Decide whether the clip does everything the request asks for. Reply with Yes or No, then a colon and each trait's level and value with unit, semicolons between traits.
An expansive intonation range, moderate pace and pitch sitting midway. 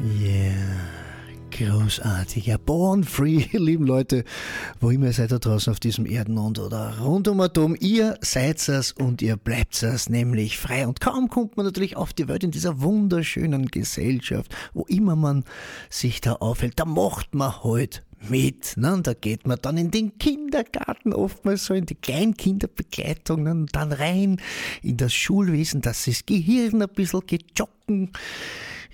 Yes: wide, 8.4 semitones; average, 165 wpm; medium, 145 Hz